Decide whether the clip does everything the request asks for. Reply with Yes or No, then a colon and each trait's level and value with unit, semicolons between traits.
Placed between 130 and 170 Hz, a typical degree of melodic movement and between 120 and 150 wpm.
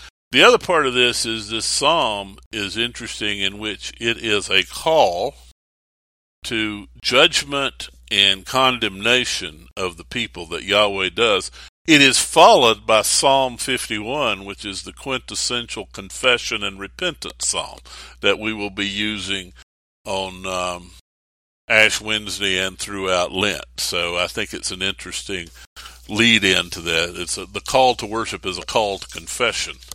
No: low, 100 Hz; average, 4.0 semitones; average, 145 wpm